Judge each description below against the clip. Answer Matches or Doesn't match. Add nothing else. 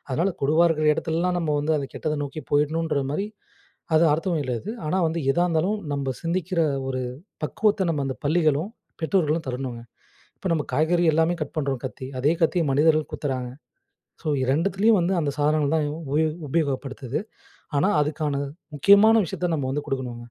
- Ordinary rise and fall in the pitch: Matches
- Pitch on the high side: Doesn't match